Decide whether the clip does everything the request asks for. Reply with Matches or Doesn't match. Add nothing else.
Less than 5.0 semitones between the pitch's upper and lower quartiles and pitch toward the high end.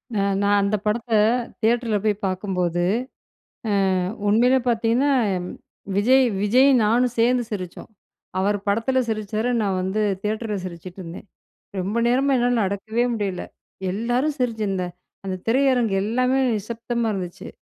Matches